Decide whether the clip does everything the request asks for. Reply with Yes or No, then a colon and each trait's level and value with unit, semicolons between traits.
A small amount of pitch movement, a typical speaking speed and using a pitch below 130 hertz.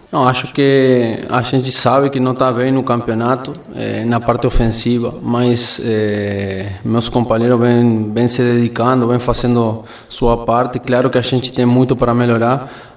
Yes: narrow, 1.4 semitones; average, 160 wpm; low, 120 Hz